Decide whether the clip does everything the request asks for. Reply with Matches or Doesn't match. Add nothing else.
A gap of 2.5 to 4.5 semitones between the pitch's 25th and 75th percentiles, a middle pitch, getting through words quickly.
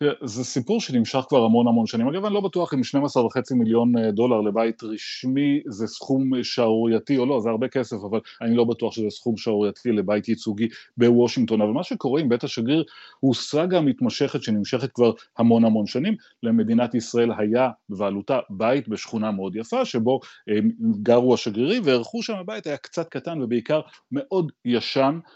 Doesn't match